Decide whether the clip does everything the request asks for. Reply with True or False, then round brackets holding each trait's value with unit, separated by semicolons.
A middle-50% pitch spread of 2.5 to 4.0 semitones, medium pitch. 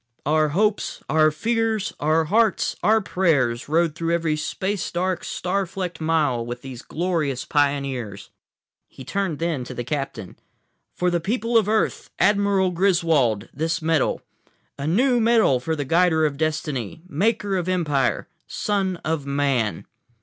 False (5.2 semitones; 165 Hz)